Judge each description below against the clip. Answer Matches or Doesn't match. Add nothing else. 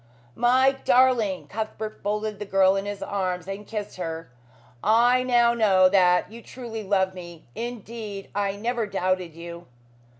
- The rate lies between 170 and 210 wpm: Doesn't match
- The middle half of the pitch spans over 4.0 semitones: Doesn't match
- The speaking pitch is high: Matches